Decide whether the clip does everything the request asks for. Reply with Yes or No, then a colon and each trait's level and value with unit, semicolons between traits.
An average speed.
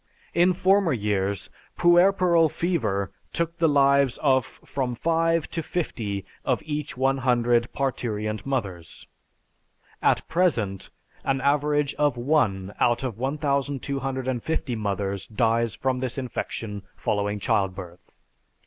No: slow, 115 wpm